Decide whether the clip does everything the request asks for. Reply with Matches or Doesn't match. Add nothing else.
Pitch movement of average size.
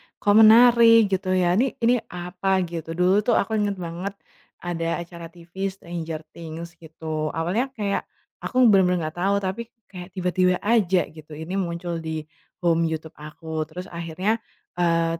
Matches